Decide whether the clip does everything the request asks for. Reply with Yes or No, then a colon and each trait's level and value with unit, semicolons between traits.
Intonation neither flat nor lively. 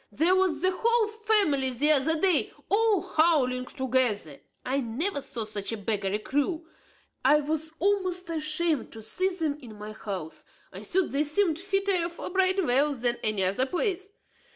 No: wide, 6.8 semitones